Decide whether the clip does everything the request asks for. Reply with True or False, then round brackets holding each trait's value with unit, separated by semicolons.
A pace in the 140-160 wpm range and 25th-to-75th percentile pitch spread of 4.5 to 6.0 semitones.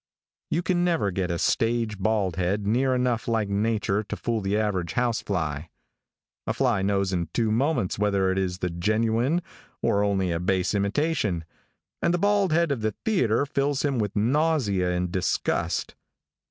False (170 wpm; 5.1 semitones)